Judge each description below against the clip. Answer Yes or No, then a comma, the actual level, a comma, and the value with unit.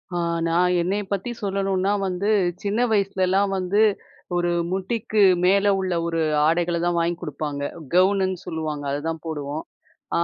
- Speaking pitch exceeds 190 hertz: No, medium, 185 Hz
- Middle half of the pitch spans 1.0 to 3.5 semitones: Yes, average, 2.9 semitones